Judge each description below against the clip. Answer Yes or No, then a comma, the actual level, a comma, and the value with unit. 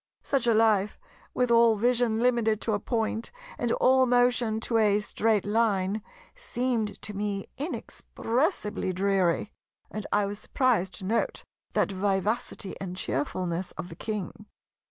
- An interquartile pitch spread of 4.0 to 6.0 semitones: No, average, 3.1 semitones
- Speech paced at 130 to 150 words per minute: Yes, average, 140 wpm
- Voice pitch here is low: No, high, 215 Hz